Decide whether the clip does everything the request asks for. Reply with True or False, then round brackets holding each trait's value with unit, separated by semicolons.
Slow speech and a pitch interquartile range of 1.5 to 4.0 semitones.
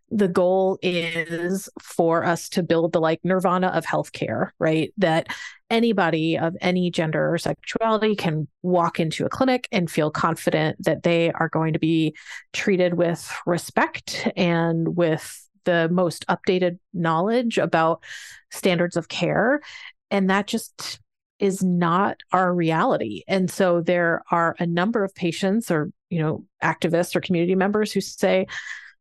False (145 wpm; 2.6 semitones)